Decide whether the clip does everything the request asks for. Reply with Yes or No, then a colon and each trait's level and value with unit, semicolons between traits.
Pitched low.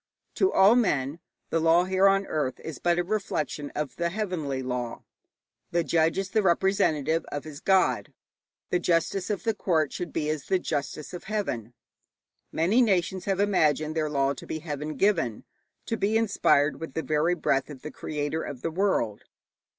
No: medium, 165 Hz